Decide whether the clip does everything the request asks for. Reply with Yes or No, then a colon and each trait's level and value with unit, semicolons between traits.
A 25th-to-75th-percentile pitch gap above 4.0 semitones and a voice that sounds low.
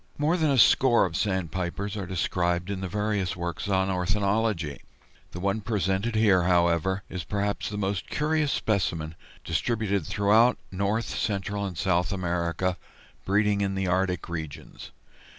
No: average, 2.7 semitones; very low, 95 Hz